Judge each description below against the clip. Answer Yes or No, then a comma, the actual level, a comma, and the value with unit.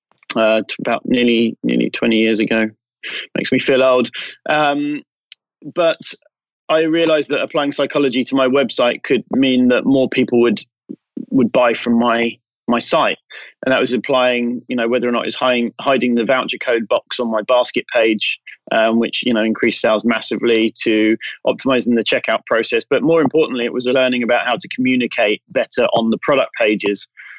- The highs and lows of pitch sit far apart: No, narrow, 2.5 semitones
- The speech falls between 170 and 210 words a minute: Yes, average, 175 wpm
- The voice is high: No, low, 120 Hz